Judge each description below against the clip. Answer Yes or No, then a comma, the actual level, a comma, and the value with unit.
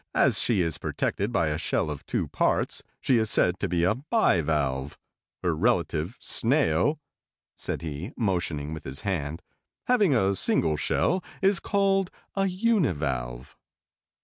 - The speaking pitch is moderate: No, very low, 90 Hz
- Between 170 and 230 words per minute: No, average, 150 wpm